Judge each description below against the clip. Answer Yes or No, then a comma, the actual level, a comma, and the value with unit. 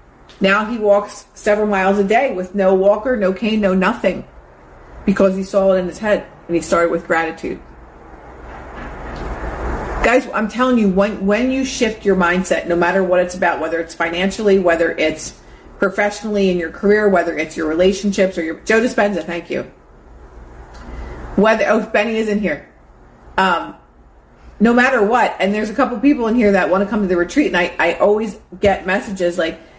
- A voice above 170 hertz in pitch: Yes, high, 190 Hz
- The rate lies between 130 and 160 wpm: No, average, 185 wpm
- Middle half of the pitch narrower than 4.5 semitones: Yes, average, 3.8 semitones